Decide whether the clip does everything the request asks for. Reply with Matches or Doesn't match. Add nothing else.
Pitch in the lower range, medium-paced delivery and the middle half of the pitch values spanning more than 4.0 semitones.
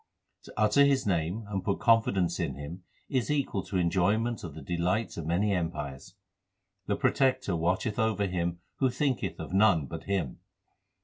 Matches